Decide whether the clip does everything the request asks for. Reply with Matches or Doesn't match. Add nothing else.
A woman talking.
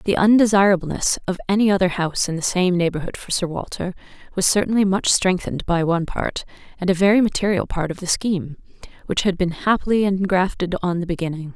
Matches